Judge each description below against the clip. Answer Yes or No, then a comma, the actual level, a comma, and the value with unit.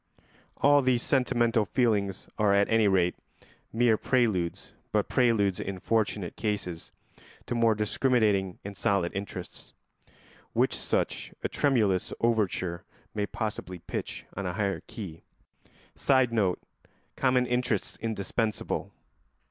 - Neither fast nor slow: No, slow, 115 wpm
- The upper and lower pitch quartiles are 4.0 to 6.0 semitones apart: No, average, 3.5 semitones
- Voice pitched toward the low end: Yes, low, 105 Hz